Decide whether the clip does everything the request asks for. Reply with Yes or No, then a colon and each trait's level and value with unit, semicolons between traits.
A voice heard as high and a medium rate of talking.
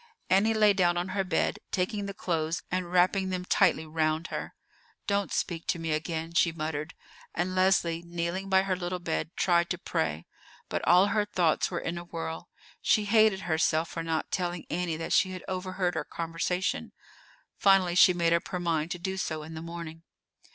No: medium, 175 Hz; average, 190 wpm